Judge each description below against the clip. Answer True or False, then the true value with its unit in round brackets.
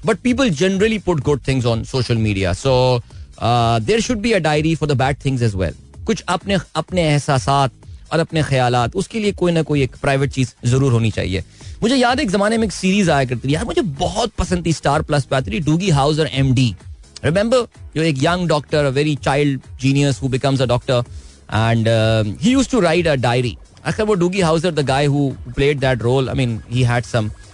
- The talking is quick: True (210 wpm)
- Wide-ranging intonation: True (5.7 semitones)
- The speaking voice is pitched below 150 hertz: True (140 Hz)